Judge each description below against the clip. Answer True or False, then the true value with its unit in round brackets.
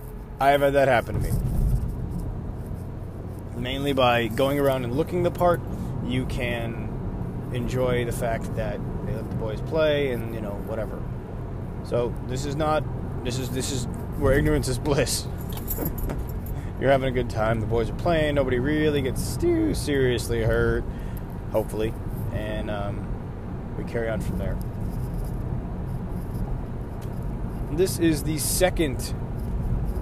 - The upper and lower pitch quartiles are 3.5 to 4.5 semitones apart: True (3.9 semitones)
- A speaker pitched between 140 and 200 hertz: False (120 Hz)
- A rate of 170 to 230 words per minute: False (140 wpm)